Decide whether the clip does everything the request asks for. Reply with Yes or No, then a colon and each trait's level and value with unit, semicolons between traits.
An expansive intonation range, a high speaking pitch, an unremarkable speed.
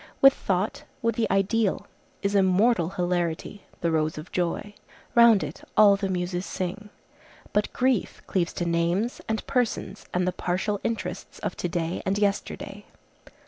No: average, 3.0 semitones; high, 195 Hz; average, 150 wpm